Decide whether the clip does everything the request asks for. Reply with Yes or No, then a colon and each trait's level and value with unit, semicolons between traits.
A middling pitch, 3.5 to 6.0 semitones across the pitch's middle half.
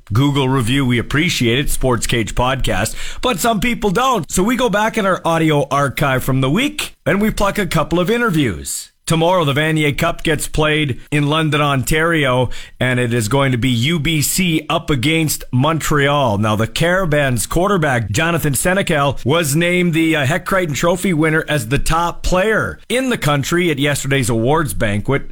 Yes: medium, 150 Hz; average, 4.5 semitones